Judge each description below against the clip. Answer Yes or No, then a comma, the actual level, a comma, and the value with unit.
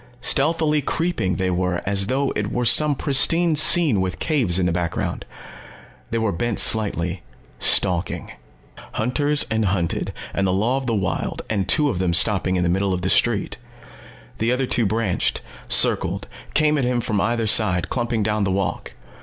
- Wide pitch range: Yes, wide, 5.9 semitones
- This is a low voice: Yes, low, 110 Hz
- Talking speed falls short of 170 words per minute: No, average, 175 wpm